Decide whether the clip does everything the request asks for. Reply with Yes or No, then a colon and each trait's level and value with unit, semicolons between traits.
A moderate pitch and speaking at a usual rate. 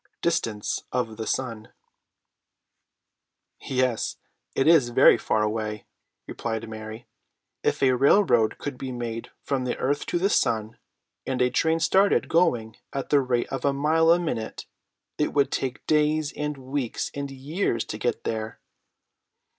No: low, 130 Hz; average, 145 wpm